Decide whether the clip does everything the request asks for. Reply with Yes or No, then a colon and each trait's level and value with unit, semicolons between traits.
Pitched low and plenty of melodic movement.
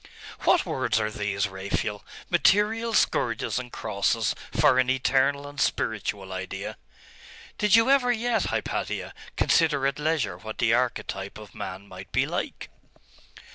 Yes: low, 125 Hz; wide, 7.1 semitones